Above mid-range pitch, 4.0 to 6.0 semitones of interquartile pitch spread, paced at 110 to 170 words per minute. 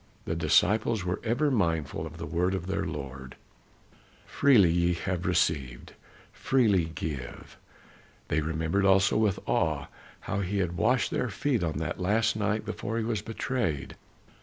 No: very low, 95 Hz; average, 5.1 semitones; average, 150 wpm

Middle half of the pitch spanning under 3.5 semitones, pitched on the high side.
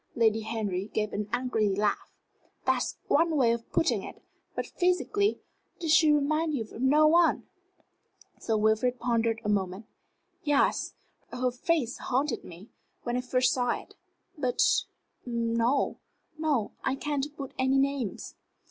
No: average, 4.8 semitones; very high, 250 Hz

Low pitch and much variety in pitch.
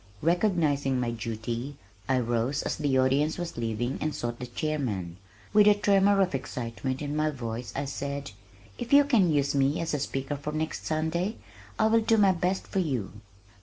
No: medium, 145 Hz; wide, 5.7 semitones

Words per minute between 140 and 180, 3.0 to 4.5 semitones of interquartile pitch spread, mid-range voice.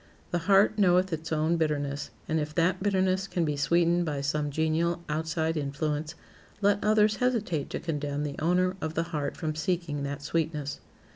Yes: average, 170 wpm; average, 3.3 semitones; medium, 160 Hz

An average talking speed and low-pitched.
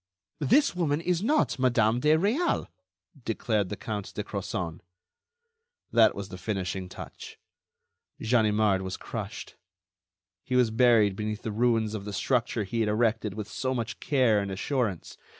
Yes: average, 150 wpm; low, 110 Hz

